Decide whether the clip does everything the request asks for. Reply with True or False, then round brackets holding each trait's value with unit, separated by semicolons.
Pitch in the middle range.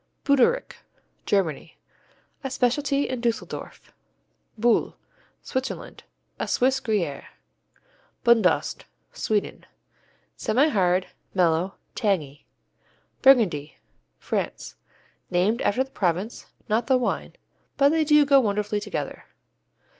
False (225 Hz)